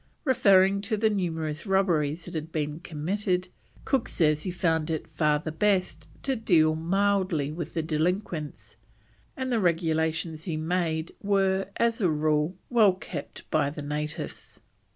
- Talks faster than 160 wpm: No, average, 150 wpm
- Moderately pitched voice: Yes, medium, 170 Hz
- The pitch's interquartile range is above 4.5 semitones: No, average, 3.8 semitones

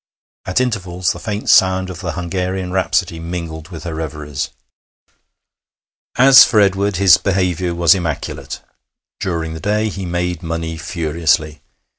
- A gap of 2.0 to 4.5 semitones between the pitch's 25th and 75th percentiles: Yes, average, 2.7 semitones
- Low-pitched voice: Yes, very low, 90 Hz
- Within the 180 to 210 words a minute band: No, slow, 135 wpm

